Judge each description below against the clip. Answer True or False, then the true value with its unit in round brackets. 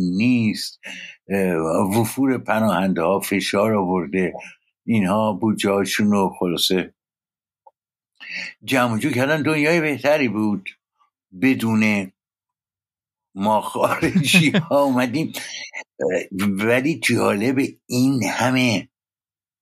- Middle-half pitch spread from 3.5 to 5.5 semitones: True (5.0 semitones)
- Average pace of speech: False (75 wpm)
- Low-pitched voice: True (110 Hz)